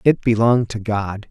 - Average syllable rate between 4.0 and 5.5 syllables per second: Yes, 5.0 syllables/s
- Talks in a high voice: No, low, 110 Hz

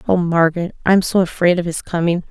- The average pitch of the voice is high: No, medium, 175 Hz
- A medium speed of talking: No, fast, 210 wpm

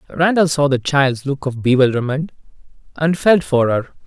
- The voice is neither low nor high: Yes, medium, 145 Hz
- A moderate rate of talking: Yes, average, 160 wpm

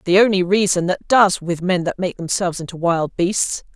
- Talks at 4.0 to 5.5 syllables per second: Yes, 5.1 syllables/s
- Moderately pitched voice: Yes, medium, 180 Hz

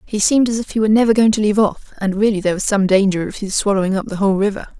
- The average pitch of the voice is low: No, high, 205 Hz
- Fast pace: Yes, fast, 300 wpm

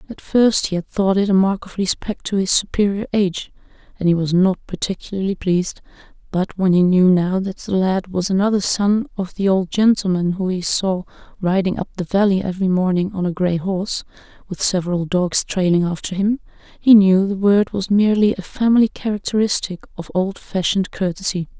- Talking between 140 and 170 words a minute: No, average, 180 wpm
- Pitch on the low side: No, high, 190 Hz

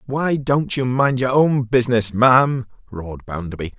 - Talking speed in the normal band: Yes, average, 160 wpm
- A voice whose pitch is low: Yes, low, 125 Hz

